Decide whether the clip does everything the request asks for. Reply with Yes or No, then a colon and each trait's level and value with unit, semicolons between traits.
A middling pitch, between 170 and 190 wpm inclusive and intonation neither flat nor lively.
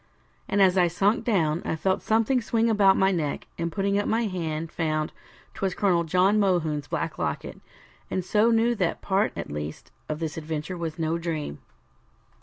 Yes: medium, 180 Hz; average, 180 wpm; average, 4.1 semitones